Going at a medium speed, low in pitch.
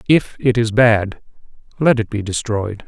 Yes: average, 165 wpm; low, 115 Hz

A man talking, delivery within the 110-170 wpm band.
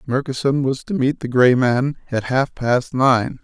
No: male; average, 190 wpm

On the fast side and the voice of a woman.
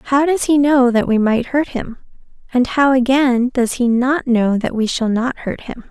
Yes: fast, 225 wpm; female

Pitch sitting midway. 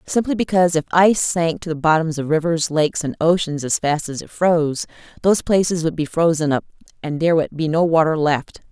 Yes: medium, 165 Hz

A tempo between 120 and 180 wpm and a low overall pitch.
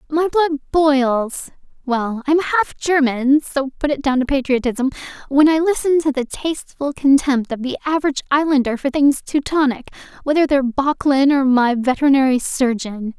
No: average, 145 wpm; very high, 275 Hz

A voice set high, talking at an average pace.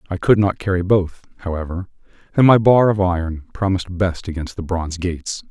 No: very low, 90 Hz; average, 185 wpm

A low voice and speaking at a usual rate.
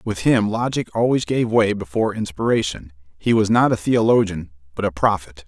Yes: low, 100 Hz; average, 175 wpm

